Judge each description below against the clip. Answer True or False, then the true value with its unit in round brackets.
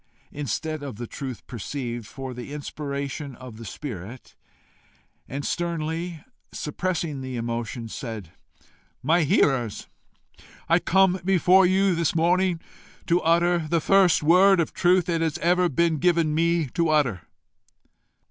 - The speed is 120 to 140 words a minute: True (135 wpm)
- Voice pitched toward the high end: False (155 Hz)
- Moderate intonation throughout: True (4.8 semitones)